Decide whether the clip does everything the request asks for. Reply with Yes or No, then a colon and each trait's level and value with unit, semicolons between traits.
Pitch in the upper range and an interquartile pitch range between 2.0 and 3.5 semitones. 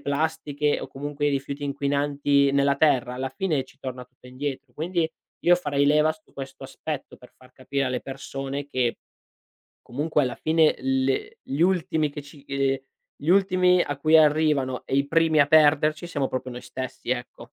No: medium, 140 Hz; narrow, 2.5 semitones